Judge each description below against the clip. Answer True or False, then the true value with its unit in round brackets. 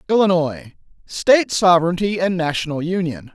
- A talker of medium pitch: True (175 Hz)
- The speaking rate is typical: False (90 wpm)